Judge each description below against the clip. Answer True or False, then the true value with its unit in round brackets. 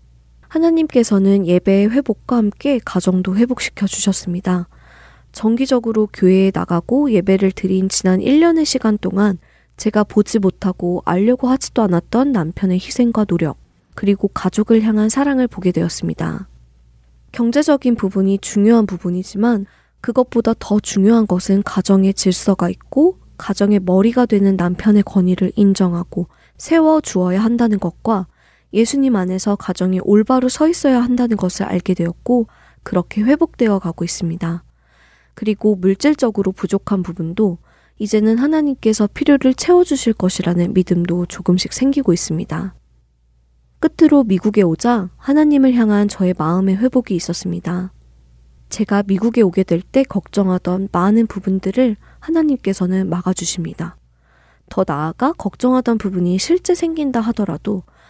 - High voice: True (200 Hz)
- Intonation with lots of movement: False (4.6 semitones)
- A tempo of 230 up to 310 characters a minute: False (325 characters per minute)